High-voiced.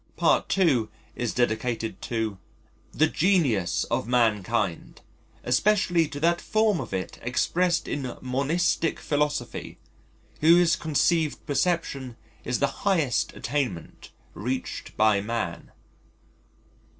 No: low, 135 Hz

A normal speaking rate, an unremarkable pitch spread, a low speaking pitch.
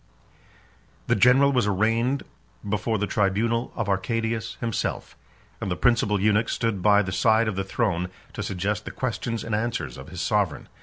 Yes: average, 165 wpm; average, 3.0 semitones; low, 105 Hz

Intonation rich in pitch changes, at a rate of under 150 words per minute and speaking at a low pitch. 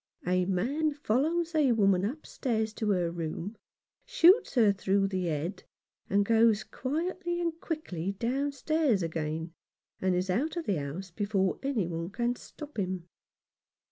No: wide, 7.9 semitones; average, 140 wpm; high, 210 Hz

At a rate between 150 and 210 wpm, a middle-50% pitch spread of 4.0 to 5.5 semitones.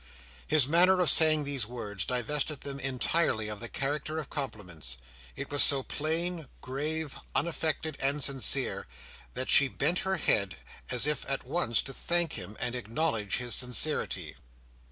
Yes: average, 155 wpm; average, 4.3 semitones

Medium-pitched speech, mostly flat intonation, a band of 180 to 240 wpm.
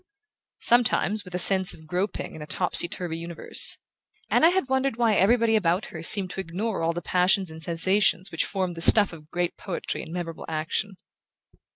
No: medium, 180 Hz; average, 3.9 semitones; average, 185 wpm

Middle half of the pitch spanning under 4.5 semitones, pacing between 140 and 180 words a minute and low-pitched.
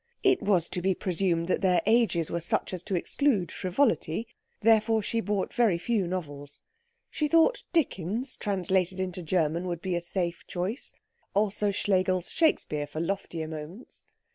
No: average, 4.0 semitones; average, 155 wpm; medium, 185 Hz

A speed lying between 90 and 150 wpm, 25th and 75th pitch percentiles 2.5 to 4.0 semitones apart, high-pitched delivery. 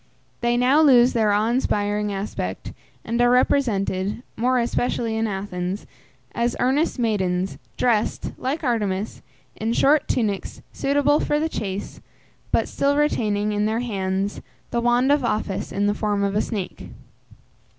Yes: average, 145 wpm; average, 3.6 semitones; high, 225 Hz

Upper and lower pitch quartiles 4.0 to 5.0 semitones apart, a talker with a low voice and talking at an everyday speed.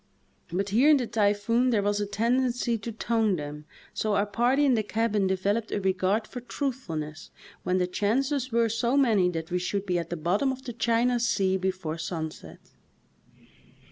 No: average, 4.3 semitones; high, 210 Hz; average, 180 wpm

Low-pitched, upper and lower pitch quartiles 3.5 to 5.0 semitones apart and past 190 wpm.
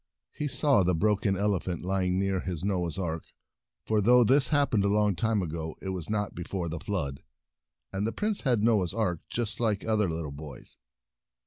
Yes: low, 100 Hz; average, 3.8 semitones; average, 200 wpm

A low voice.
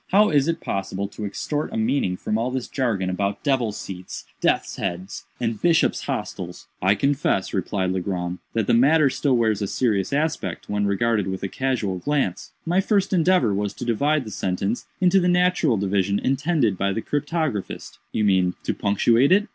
Yes: low, 115 Hz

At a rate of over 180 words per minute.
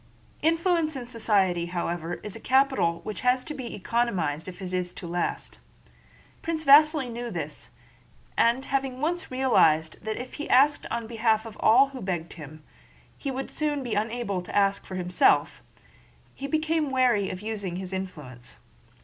No: average, 165 wpm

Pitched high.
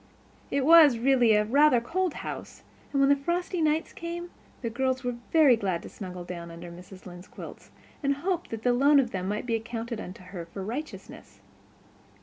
Yes: high, 245 Hz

